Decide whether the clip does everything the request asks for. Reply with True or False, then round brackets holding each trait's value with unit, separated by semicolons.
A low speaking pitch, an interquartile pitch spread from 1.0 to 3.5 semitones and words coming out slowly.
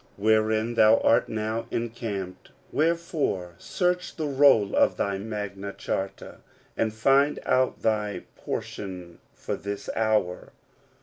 True (110 Hz; 3.0 semitones; 120 wpm)